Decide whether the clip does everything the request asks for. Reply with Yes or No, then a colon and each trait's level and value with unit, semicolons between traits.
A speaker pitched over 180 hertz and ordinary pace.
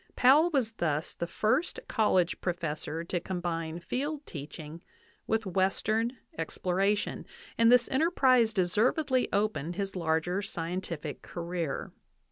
No: high, 190 Hz; slow, 110 wpm